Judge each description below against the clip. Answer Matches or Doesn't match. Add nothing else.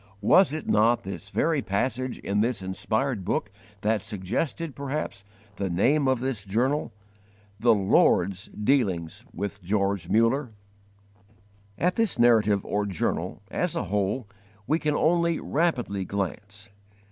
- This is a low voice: Matches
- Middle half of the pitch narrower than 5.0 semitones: Doesn't match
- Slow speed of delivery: Matches